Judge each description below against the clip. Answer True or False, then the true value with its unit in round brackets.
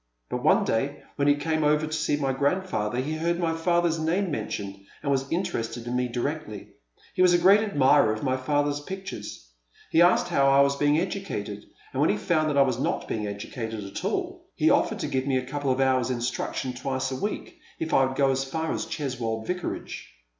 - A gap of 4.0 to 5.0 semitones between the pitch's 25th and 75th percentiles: True (4.3 semitones)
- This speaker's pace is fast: True (220 wpm)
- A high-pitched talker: False (140 Hz)